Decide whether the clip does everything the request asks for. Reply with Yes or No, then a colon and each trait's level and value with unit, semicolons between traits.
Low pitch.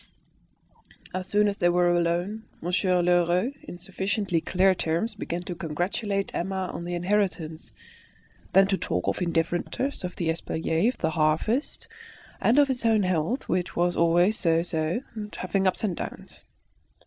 No: medium, 180 Hz